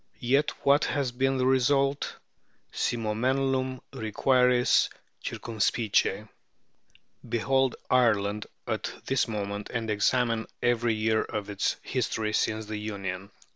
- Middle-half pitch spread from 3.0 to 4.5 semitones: Yes, average, 3.4 semitones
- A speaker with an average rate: No, slow, 110 wpm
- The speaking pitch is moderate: No, low, 115 Hz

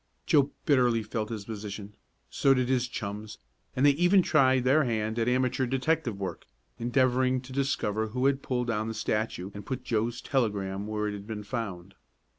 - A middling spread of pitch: Yes, average, 3.6 semitones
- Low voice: Yes, low, 120 Hz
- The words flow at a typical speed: Yes, average, 180 wpm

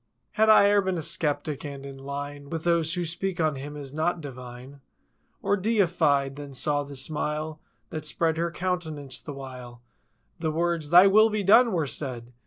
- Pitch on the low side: No, medium, 155 Hz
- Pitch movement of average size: Yes, average, 3.7 semitones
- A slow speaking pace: No, average, 180 wpm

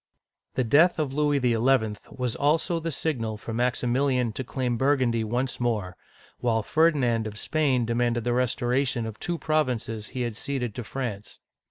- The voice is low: Yes, low, 125 Hz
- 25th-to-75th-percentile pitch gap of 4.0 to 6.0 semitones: No, average, 3.5 semitones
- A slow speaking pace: No, average, 165 wpm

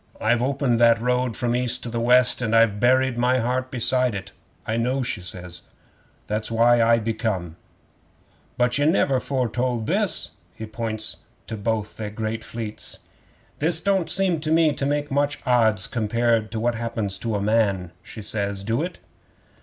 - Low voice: Yes, low, 115 Hz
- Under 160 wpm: No, average, 175 wpm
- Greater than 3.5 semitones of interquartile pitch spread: No, average, 2.7 semitones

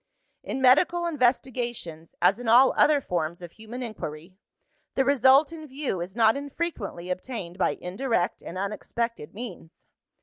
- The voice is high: Yes, high, 235 Hz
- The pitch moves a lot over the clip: Yes, wide, 6.6 semitones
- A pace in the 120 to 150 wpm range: Yes, average, 140 wpm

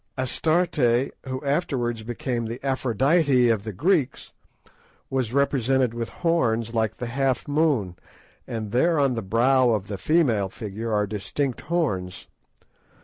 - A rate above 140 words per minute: No, slow, 135 wpm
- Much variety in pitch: No, average, 3.9 semitones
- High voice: No, low, 125 Hz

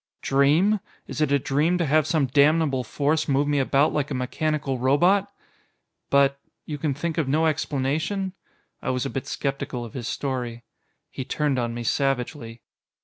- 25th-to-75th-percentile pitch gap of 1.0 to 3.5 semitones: Yes, average, 2.9 semitones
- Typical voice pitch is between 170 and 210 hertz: No, medium, 140 Hz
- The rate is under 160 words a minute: No, average, 170 wpm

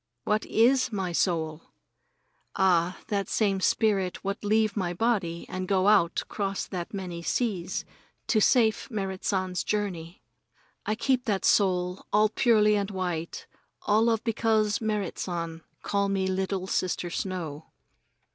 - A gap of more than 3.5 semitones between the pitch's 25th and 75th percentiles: No, average, 2.9 semitones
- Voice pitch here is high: Yes, high, 195 Hz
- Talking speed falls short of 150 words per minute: Yes, slow, 135 wpm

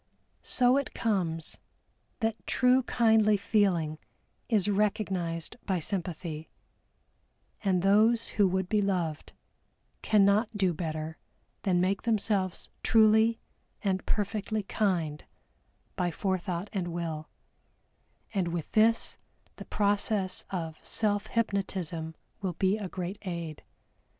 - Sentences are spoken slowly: Yes, slow, 110 wpm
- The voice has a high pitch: Yes, high, 195 Hz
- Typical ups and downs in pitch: Yes, average, 3.6 semitones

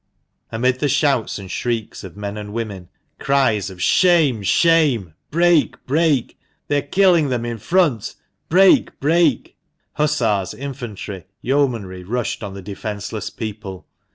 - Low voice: Yes, low, 120 Hz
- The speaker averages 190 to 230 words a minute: No, average, 145 wpm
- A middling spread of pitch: No, wide, 6.1 semitones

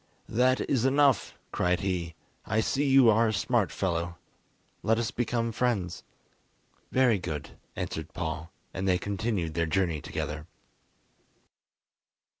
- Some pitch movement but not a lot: No, wide, 5.7 semitones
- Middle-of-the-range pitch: No, very low, 95 Hz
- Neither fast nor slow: No, slow, 125 wpm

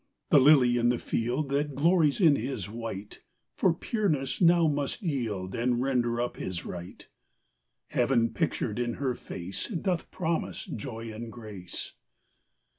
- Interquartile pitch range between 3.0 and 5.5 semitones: Yes, average, 4.4 semitones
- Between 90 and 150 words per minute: Yes, average, 140 wpm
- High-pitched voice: No, low, 125 Hz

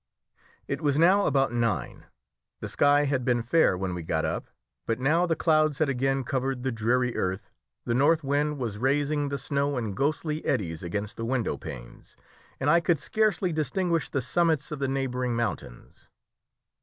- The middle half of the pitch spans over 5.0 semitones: No, average, 4.4 semitones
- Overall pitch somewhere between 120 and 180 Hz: Yes, low, 135 Hz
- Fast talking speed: No, average, 175 wpm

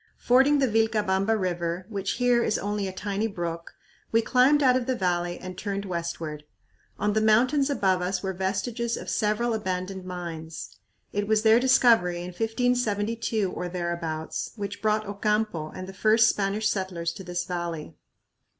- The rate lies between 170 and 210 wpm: No, average, 160 wpm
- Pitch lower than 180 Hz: No, high, 200 Hz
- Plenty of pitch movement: No, average, 3.9 semitones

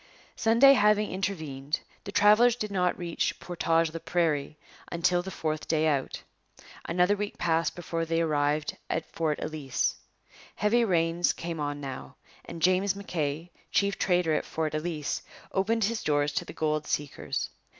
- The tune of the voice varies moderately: Yes, average, 4.2 semitones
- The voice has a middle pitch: Yes, medium, 165 Hz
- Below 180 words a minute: Yes, average, 150 wpm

